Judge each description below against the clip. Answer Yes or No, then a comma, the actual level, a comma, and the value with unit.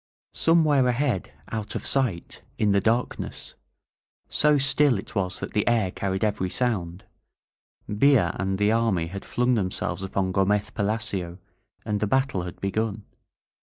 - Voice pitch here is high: No, low, 105 Hz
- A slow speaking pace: No, average, 160 wpm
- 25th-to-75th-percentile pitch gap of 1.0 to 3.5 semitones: No, average, 4.2 semitones